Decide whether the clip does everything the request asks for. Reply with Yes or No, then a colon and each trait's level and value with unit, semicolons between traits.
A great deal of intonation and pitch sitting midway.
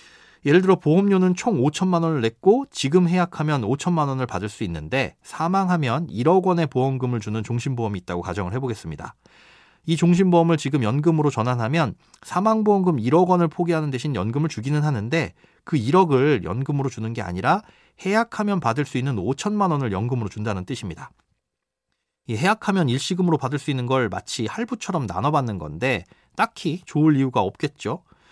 Yes: wide, 6.2 semitones; medium, 150 Hz